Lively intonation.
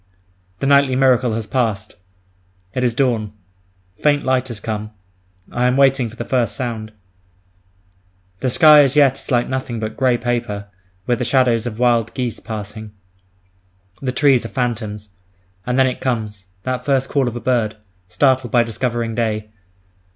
No: average, 3.0 semitones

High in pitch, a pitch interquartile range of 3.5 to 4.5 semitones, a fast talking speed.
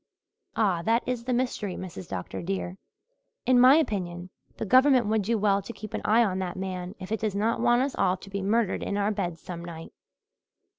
Yes: high, 205 Hz; average, 4.0 semitones; fast, 210 wpm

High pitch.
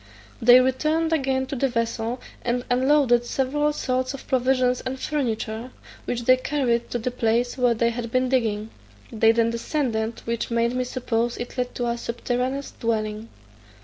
Yes: high, 245 Hz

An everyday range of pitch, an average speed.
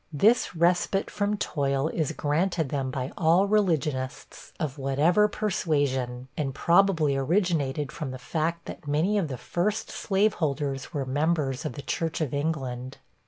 Yes: average, 4.4 semitones; average, 145 wpm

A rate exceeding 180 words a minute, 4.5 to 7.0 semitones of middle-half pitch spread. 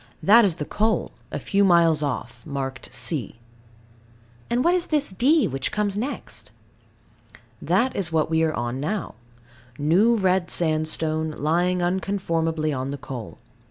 No: average, 145 wpm; average, 5.1 semitones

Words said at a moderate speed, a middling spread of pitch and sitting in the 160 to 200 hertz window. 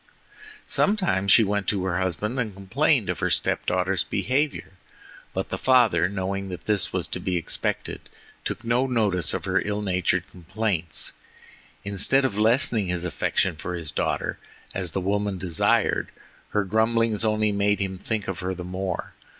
No: average, 165 wpm; average, 3.0 semitones; low, 100 Hz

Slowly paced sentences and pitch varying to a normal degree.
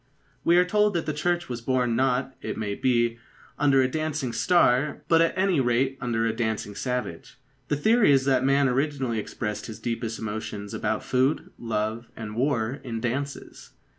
No: average, 175 wpm; average, 4.1 semitones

